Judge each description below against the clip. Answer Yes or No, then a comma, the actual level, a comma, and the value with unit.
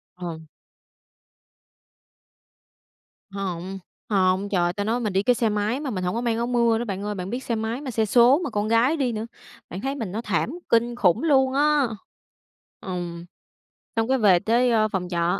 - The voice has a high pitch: Yes, high, 220 Hz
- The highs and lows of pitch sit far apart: No, average, 4.2 semitones